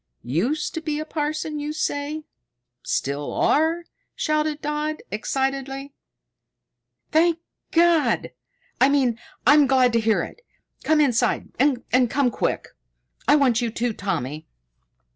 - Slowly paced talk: Yes, slow, 125 wpm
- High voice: Yes, very high, 285 Hz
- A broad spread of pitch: No, average, 3.9 semitones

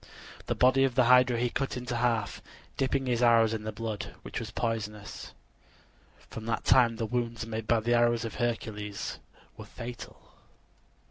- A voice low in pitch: Yes, low, 115 Hz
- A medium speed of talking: Yes, average, 165 wpm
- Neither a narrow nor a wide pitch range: No, narrow, 1.7 semitones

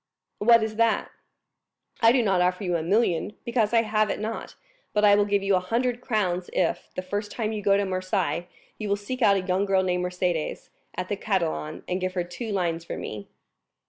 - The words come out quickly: Yes, fast, 215 wpm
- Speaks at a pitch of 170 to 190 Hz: No, high, 200 Hz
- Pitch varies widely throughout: No, average, 3.0 semitones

